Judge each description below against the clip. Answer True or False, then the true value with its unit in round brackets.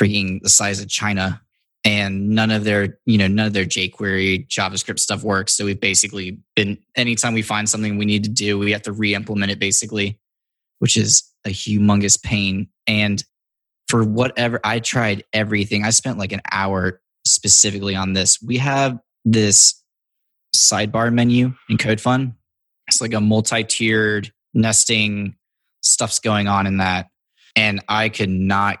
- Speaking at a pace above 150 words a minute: True (160 wpm)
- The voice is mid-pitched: False (105 Hz)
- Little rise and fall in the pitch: True (2.0 semitones)